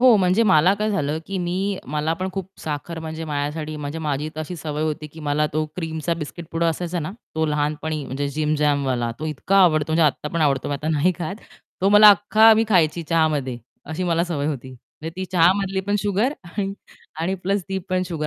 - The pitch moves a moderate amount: Yes, average, 3.6 semitones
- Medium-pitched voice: Yes, medium, 160 Hz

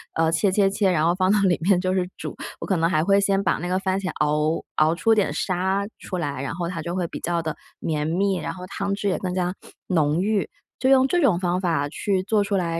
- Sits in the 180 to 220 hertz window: Yes, medium, 185 Hz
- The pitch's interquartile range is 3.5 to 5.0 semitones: No, average, 2.9 semitones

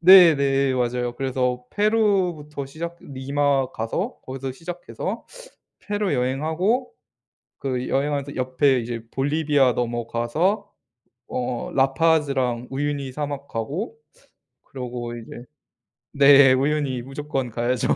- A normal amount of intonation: Yes, average, 3.2 semitones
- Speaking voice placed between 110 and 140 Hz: Yes, low, 135 Hz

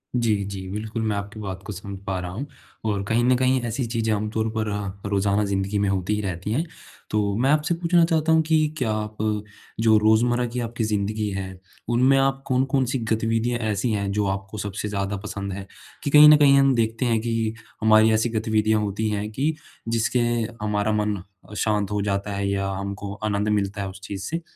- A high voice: No, low, 110 Hz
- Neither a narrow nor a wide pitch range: Yes, average, 3.1 semitones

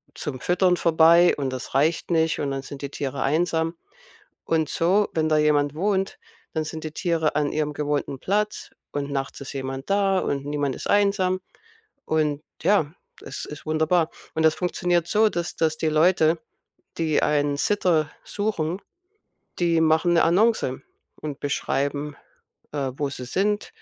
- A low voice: No, medium, 160 Hz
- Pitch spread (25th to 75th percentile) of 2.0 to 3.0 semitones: No, average, 3.5 semitones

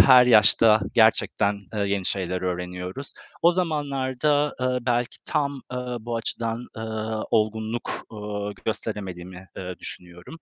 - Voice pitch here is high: No, low, 110 Hz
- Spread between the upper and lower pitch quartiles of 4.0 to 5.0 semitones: Yes, average, 4.3 semitones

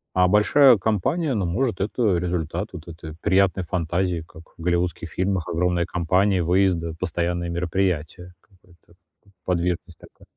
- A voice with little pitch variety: Yes, narrow, 2.0 semitones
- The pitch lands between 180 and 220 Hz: No, very low, 90 Hz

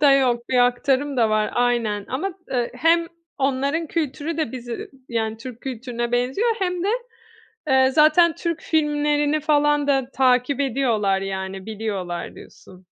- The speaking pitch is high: Yes, very high, 260 Hz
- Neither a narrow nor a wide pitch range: Yes, average, 4.1 semitones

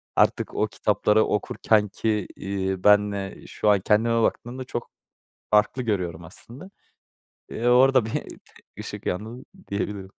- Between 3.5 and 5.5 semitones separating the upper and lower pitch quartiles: No, average, 2.9 semitones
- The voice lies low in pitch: Yes, low, 105 Hz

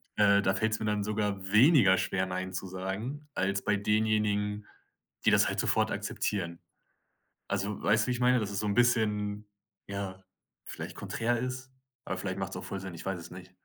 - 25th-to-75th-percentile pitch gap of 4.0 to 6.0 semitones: No, narrow, 2.4 semitones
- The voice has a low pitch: Yes, low, 105 Hz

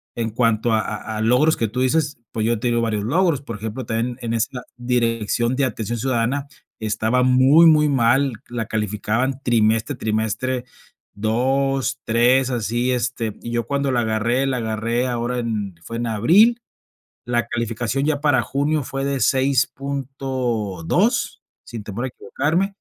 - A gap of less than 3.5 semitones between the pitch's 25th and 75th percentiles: Yes, average, 3.1 semitones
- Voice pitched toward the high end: No, low, 120 Hz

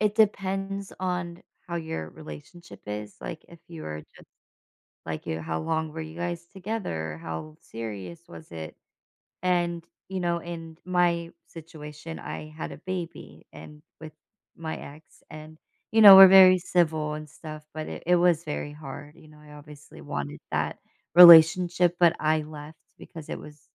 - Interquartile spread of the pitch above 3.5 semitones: No, average, 2.9 semitones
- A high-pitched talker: No, medium, 160 Hz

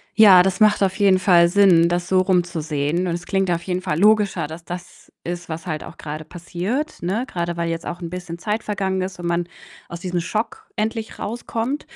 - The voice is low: No, medium, 180 Hz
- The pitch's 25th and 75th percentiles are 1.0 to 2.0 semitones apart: No, average, 2.8 semitones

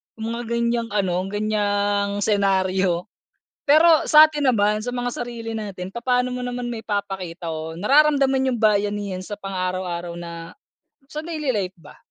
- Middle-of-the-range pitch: No, high, 210 Hz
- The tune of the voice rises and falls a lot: No, average, 4.6 semitones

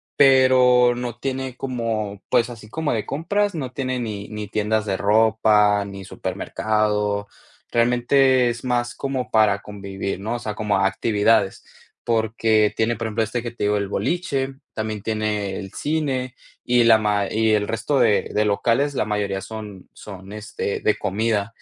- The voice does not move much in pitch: No, average, 3.0 semitones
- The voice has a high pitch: No, low, 110 Hz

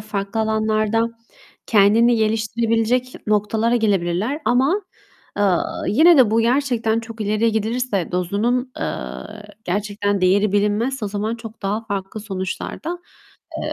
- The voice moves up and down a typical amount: No, narrow, 2.3 semitones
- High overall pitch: Yes, high, 220 Hz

